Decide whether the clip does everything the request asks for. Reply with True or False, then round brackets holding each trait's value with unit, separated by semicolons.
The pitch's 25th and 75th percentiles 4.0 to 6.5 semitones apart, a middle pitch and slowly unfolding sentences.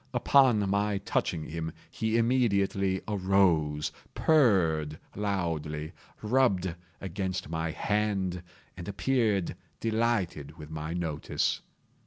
False (4.6 semitones; 95 Hz; 95 wpm)